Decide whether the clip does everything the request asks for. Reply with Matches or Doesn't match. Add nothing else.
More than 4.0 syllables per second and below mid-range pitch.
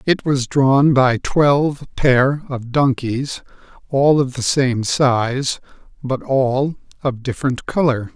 Doesn't match